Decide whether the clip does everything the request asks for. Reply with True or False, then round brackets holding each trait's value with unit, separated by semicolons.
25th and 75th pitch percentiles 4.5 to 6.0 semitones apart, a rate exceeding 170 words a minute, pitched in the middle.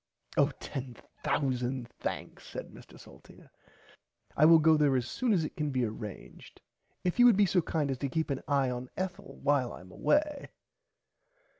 True (5.3 semitones; 180 wpm; 145 Hz)